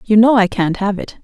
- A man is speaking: No, female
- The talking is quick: Yes, fast, 290 wpm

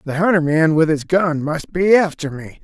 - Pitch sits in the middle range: Yes, medium, 160 Hz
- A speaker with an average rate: No, fast, 225 wpm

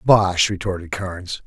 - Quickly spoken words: No, slow, 125 wpm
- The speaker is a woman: No, male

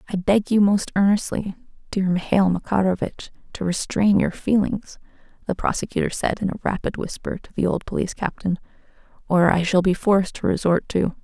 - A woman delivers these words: Yes, female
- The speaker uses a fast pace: No, average, 170 wpm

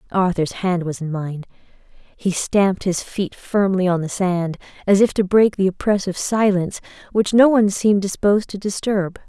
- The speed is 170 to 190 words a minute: Yes, average, 175 wpm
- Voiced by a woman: Yes, female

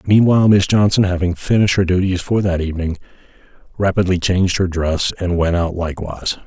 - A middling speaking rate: Yes, average, 165 wpm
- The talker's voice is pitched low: Yes, very low, 90 Hz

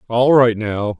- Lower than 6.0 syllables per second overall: Yes, 3.7 syllables/s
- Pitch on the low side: Yes, low, 115 Hz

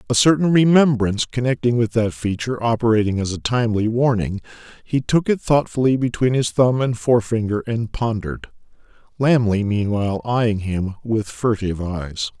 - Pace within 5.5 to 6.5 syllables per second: No, 5.2 syllables/s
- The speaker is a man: Yes, male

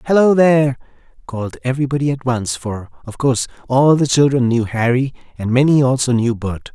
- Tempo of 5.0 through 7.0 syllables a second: Yes, 5.7 syllables/s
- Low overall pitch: Yes, low, 125 Hz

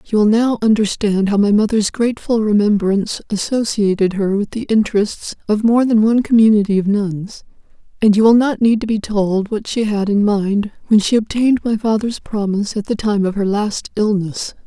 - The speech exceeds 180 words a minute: Yes, average, 190 wpm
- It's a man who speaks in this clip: No, female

